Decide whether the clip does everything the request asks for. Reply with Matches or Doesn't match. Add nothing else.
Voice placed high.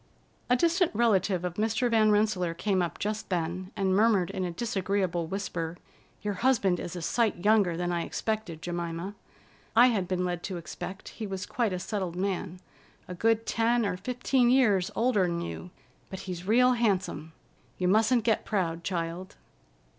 Matches